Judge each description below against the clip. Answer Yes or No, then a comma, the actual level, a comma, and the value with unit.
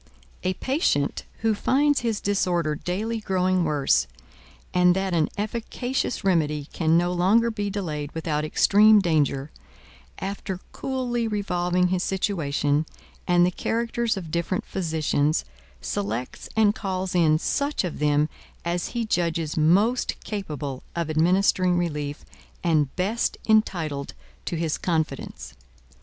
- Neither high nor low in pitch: Yes, medium, 180 Hz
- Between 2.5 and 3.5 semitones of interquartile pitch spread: No, average, 4.9 semitones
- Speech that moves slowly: Yes, slow, 125 wpm